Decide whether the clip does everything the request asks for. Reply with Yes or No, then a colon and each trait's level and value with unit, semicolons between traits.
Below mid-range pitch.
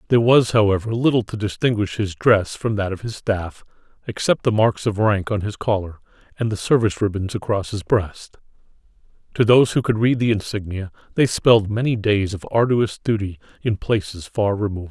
Yes: low, 105 Hz